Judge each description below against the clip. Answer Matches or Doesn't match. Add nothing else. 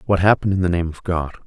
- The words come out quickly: Matches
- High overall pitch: Doesn't match